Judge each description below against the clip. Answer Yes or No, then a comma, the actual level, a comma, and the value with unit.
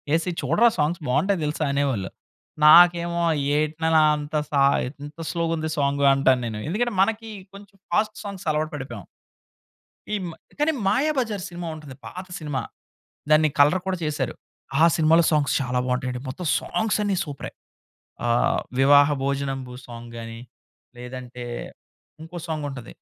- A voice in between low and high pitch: Yes, medium, 155 Hz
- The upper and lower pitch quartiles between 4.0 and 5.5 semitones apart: Yes, average, 4.8 semitones